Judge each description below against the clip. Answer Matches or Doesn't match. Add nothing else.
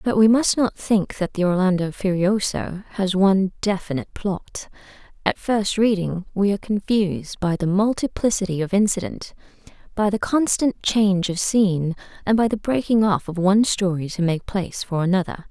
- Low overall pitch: Doesn't match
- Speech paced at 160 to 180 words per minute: Matches